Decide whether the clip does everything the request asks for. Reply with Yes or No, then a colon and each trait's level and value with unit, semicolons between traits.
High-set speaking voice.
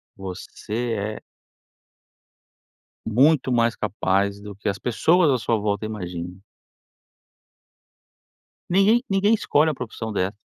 No: low, 110 Hz